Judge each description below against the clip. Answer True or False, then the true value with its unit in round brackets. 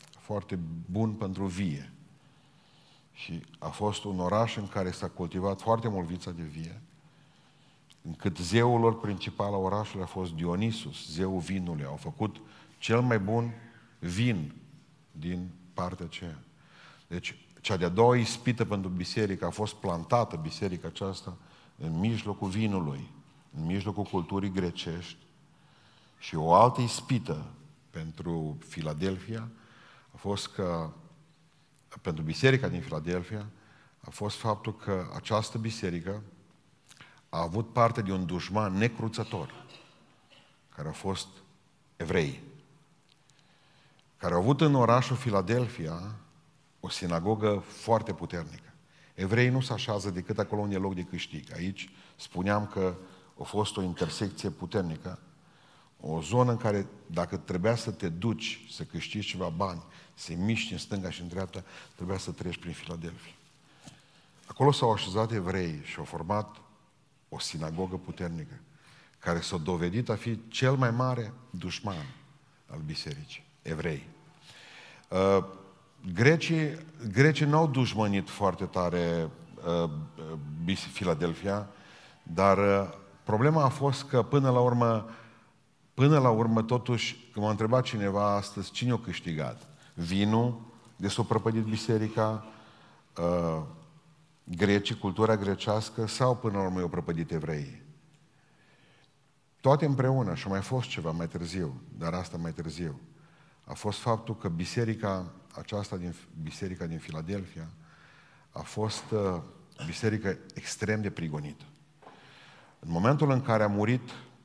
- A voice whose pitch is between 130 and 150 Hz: False (105 Hz)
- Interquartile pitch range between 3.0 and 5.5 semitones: True (5.2 semitones)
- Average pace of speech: True (125 wpm)